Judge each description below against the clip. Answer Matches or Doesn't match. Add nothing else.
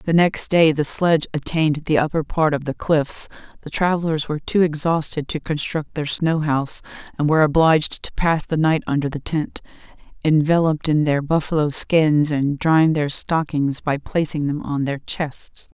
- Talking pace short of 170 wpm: Doesn't match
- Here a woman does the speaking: Matches